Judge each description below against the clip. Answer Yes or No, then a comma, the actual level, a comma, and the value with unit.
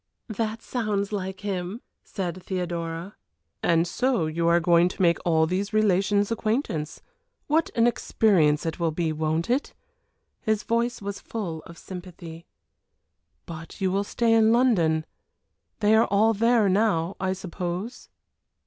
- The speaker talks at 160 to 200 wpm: No, average, 140 wpm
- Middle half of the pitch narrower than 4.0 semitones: No, average, 4.4 semitones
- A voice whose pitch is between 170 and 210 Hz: Yes, high, 190 Hz